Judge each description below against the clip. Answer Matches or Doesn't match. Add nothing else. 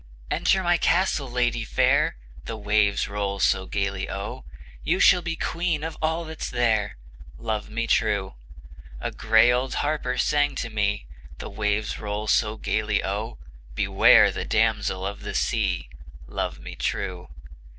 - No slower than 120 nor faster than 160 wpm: Matches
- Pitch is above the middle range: Doesn't match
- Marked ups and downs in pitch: Doesn't match